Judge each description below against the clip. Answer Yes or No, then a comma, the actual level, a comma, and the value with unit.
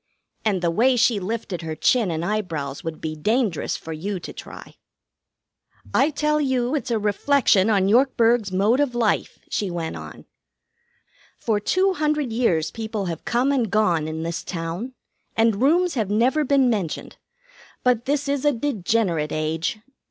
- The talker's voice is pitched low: No, high, 220 Hz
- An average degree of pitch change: No, wide, 6.8 semitones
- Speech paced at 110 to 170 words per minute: Yes, average, 160 wpm